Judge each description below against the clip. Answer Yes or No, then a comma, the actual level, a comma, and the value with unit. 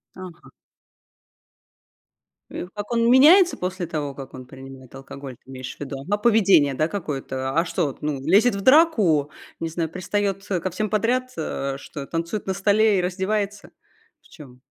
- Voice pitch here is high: No, medium, 180 Hz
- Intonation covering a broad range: Yes, wide, 6.5 semitones